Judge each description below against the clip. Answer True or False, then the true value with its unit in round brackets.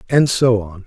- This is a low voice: True (115 Hz)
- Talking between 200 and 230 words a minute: True (210 wpm)